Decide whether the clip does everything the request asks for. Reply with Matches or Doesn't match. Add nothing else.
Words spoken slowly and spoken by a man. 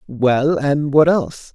Matches